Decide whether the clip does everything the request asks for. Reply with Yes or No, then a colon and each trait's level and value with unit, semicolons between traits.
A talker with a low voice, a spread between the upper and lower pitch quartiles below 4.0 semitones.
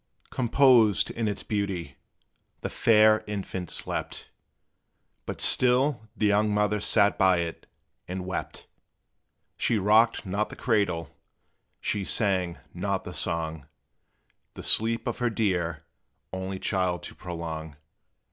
Yes: low, 100 Hz; average, 3.5 semitones